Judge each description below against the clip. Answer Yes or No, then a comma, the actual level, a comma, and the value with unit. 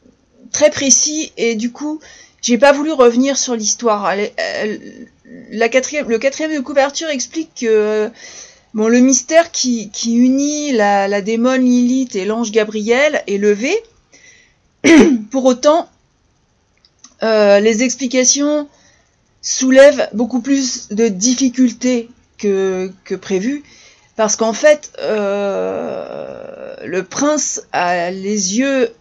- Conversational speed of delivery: No, slow, 120 wpm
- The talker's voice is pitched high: Yes, very high, 255 Hz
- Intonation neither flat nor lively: Yes, average, 5.0 semitones